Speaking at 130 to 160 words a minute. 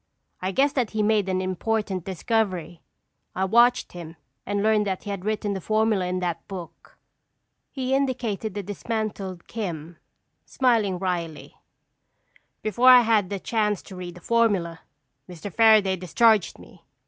Yes: average, 150 wpm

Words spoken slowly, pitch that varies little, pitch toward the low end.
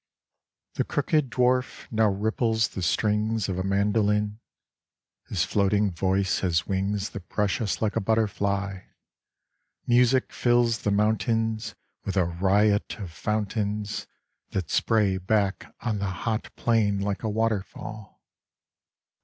Yes: slow, 125 wpm; narrow, 2.2 semitones; low, 105 Hz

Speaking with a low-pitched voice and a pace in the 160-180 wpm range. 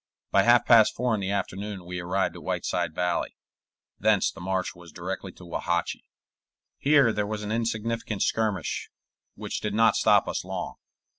Yes: low, 100 Hz; average, 165 wpm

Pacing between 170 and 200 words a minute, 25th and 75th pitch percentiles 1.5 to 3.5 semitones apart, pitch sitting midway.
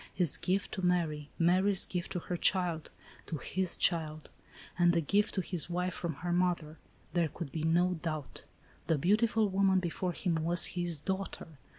Yes: average, 175 wpm; narrow, 2.4 semitones; medium, 175 Hz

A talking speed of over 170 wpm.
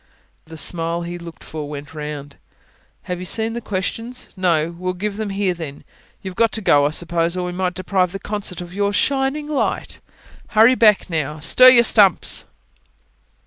Yes: average, 180 wpm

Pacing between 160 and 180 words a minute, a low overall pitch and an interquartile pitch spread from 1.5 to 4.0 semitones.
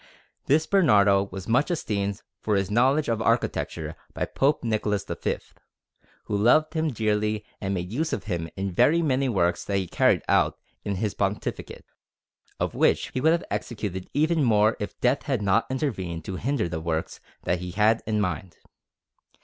No: average, 175 wpm; low, 105 Hz; average, 5.3 semitones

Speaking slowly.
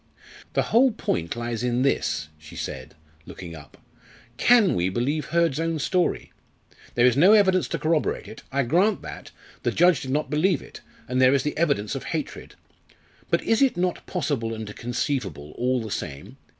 No: average, 175 wpm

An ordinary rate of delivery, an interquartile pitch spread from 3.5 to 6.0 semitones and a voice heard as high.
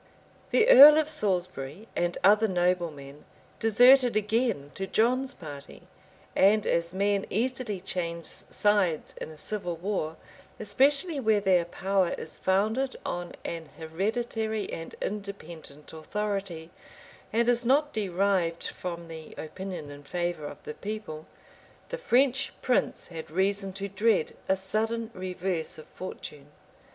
No: slow, 130 wpm; average, 4.7 semitones; high, 195 Hz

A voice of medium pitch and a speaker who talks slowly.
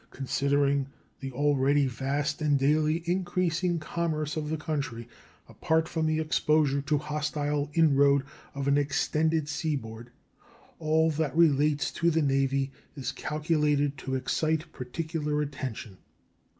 Yes: medium, 150 Hz; slow, 125 wpm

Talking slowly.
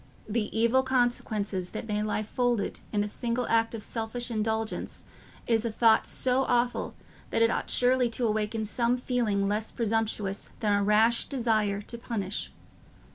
No: average, 160 wpm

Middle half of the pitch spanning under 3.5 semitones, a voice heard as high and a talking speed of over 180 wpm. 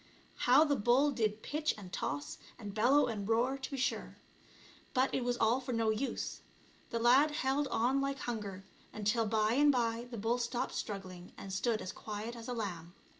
No: average, 3.8 semitones; high, 235 Hz; average, 190 wpm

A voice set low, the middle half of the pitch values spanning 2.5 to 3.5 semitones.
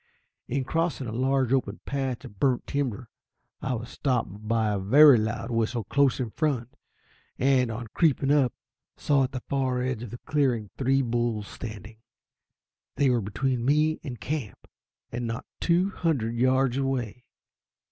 Yes: low, 125 Hz; average, 3.1 semitones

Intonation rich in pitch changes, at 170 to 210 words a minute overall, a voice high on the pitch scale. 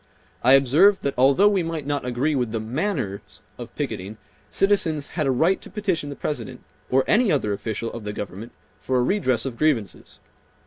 No: wide, 5.8 semitones; average, 185 wpm; low, 135 Hz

